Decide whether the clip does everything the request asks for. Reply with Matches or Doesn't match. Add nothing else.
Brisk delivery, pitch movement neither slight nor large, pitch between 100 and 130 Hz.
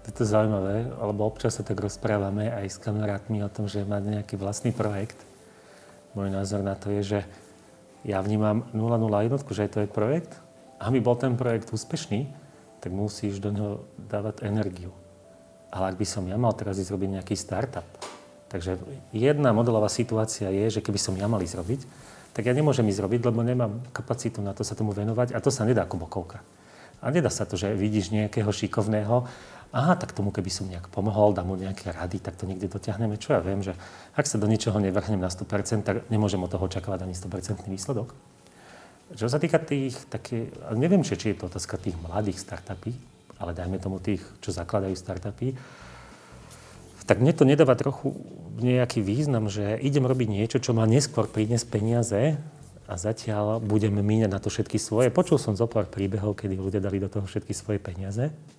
Matches